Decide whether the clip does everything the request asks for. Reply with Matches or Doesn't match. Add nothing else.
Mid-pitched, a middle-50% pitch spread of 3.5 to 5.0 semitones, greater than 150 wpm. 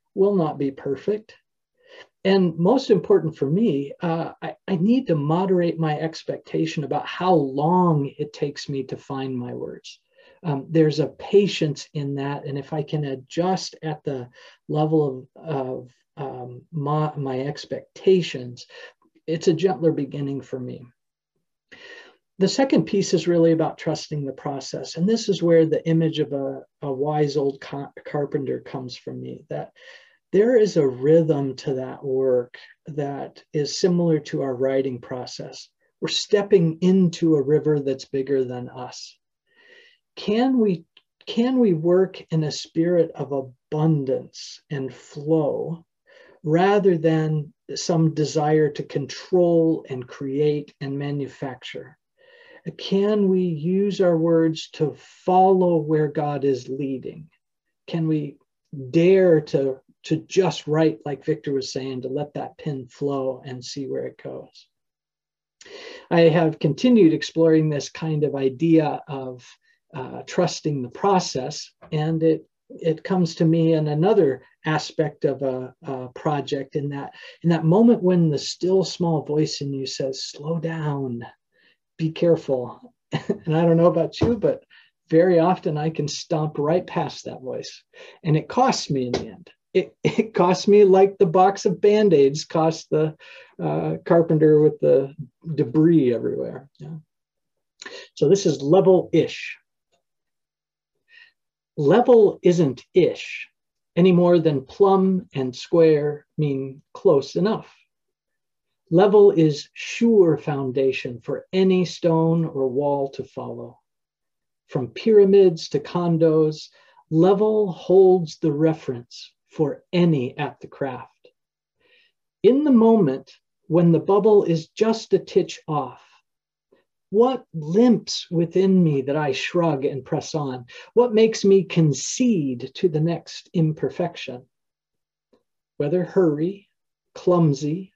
Doesn't match